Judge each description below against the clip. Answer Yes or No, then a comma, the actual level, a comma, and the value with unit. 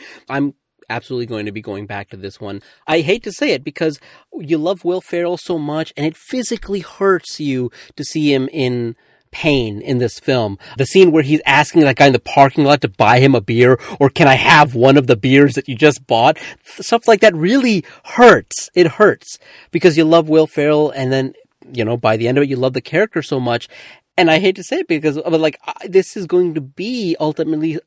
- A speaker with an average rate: No, fast, 230 wpm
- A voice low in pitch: No, medium, 150 Hz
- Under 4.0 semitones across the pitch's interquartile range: No, average, 4.7 semitones